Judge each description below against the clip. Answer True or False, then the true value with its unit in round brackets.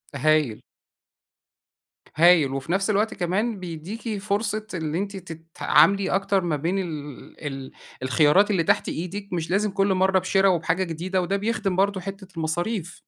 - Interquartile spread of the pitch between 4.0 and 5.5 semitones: False (3.5 semitones)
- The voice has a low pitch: False (185 Hz)